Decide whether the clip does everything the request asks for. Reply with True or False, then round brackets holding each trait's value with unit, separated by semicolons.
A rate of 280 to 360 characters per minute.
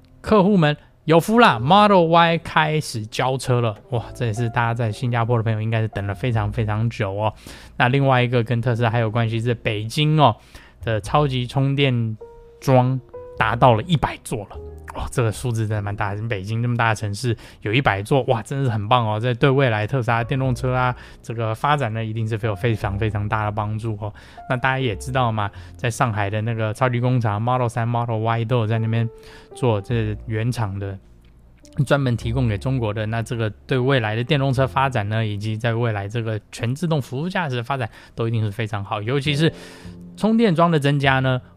True (320 characters per minute)